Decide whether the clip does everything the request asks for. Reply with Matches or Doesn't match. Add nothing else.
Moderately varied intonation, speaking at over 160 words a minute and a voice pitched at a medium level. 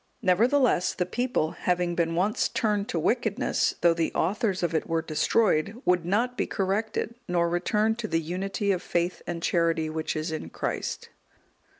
Matches